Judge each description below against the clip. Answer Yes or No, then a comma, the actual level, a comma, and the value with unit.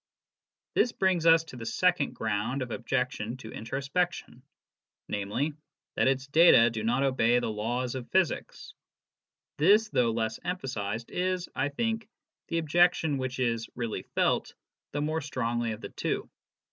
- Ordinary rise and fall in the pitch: No, wide, 6.1 semitones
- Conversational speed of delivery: Yes, average, 150 wpm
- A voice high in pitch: No, low, 130 Hz